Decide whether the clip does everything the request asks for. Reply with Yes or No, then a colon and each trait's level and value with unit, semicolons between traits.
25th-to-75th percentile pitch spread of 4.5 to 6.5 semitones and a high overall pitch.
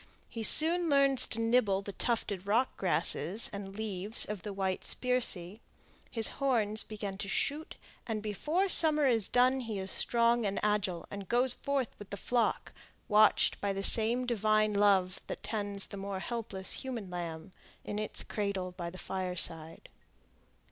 No: average, 3.6 semitones; high, 210 Hz